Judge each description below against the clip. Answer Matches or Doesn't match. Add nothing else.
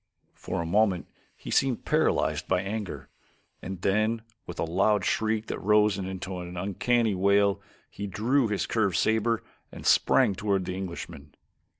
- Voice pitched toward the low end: Matches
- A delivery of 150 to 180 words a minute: Matches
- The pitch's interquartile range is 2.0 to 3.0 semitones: Matches